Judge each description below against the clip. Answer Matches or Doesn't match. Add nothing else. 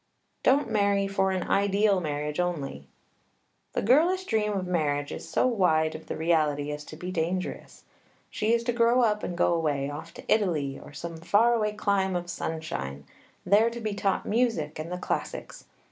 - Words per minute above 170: Matches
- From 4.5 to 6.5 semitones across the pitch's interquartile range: Matches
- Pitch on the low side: Doesn't match